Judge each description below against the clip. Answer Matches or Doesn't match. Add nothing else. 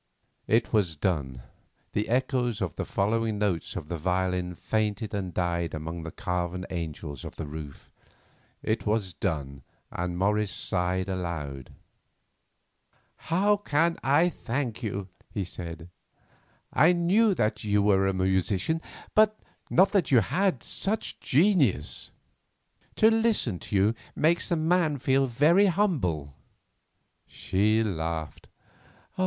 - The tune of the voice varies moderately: Doesn't match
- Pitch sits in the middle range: Doesn't match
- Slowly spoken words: Matches